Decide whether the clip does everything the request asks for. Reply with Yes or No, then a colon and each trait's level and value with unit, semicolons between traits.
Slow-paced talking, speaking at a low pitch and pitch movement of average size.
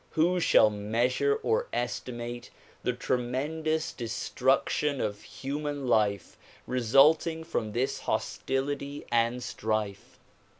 Yes: slow, 100 wpm; low, 125 Hz; average, 4.1 semitones